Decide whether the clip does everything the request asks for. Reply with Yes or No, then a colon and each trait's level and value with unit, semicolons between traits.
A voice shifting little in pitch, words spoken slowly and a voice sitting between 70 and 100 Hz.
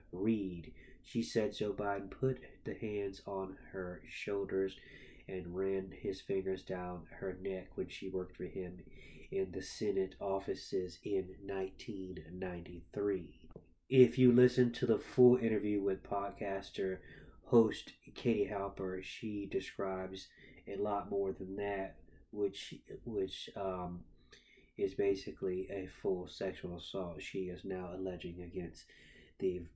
Yes: narrow, 1.7 semitones; slow, 130 wpm; very low, 95 Hz